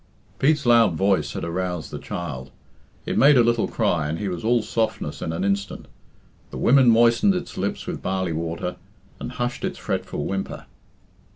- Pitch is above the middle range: No, very low, 95 Hz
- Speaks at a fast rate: No, average, 175 wpm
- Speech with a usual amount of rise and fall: No, wide, 5.8 semitones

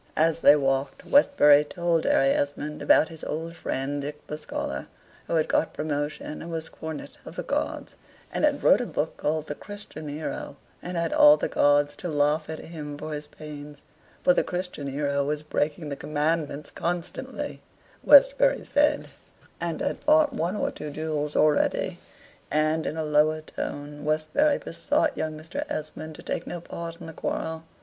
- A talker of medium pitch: Yes, medium, 155 Hz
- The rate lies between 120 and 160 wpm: No, average, 175 wpm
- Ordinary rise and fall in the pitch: No, narrow, 2.0 semitones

